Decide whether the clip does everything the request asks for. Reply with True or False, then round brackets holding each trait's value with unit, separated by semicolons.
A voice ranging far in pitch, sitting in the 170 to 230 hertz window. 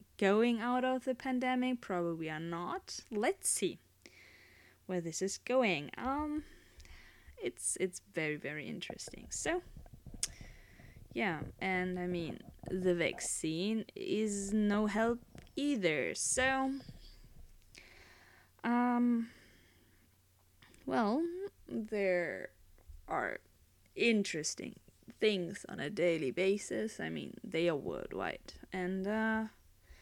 True (7.6 semitones; 190 Hz)